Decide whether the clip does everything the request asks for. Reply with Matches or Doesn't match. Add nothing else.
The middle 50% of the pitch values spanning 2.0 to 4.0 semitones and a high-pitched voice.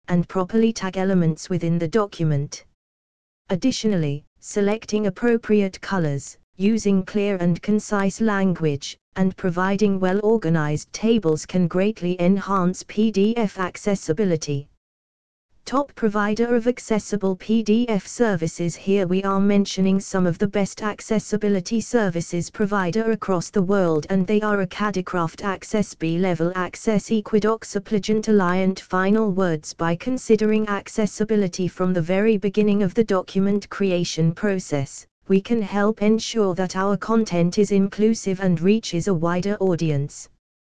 Matches